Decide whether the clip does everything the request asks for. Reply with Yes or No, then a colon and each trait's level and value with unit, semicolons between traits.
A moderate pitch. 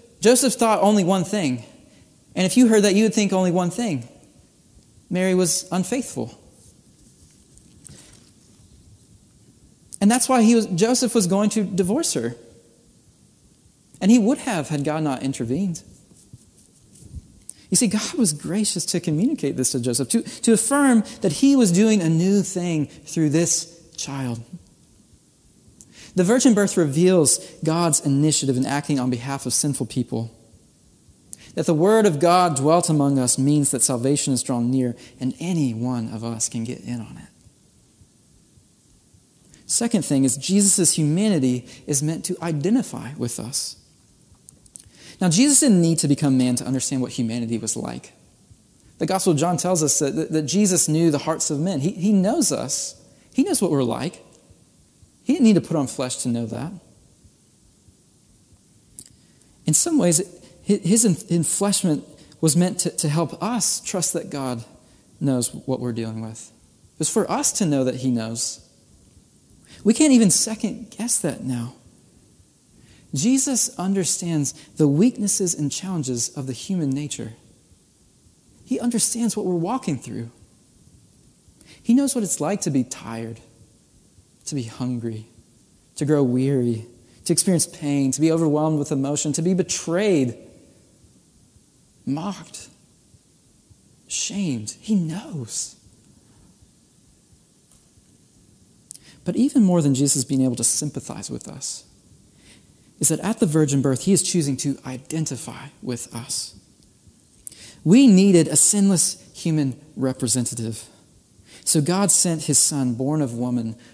Yes: medium, 155 Hz